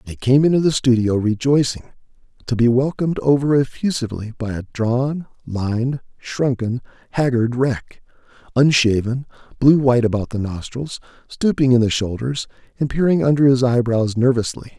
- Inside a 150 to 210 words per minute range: No, slow, 135 wpm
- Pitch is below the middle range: Yes, low, 125 Hz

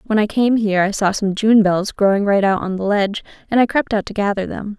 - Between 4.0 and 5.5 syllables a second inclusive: No, 6.1 syllables/s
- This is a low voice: No, high, 205 Hz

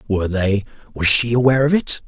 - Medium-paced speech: Yes, average, 145 wpm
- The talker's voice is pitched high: No, low, 115 Hz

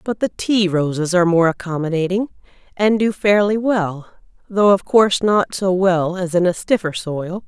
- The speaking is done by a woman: Yes, female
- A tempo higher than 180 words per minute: No, average, 175 wpm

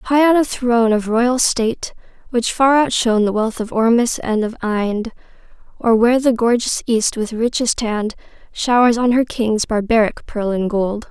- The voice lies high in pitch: Yes, high, 230 Hz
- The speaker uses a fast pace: No, average, 180 wpm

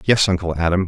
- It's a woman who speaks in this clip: No, male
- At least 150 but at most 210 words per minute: Yes, fast, 205 wpm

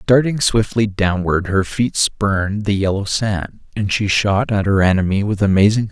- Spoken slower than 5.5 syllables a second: Yes, 4.8 syllables/s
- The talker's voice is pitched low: Yes, low, 100 Hz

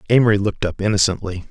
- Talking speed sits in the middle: Yes, average, 160 wpm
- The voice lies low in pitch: Yes, low, 100 Hz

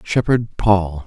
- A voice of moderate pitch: No, low, 100 Hz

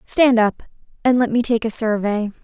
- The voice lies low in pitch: No, high, 230 Hz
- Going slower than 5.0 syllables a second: Yes, 4.8 syllables/s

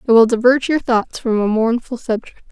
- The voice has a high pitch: Yes, high, 235 Hz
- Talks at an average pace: No, fast, 215 wpm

